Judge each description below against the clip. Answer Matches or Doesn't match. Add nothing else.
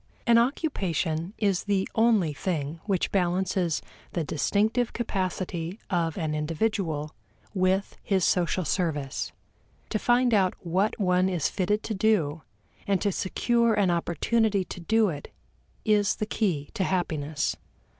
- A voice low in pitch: Doesn't match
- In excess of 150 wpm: Doesn't match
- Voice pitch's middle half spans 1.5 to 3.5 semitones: Doesn't match